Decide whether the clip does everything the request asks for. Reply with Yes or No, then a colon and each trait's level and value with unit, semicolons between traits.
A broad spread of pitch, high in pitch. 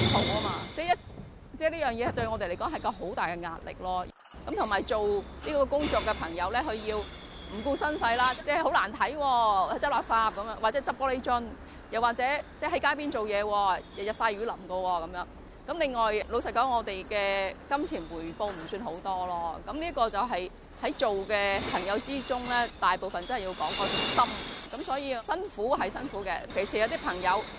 Yes: wide, 5.8 semitones; high, 225 Hz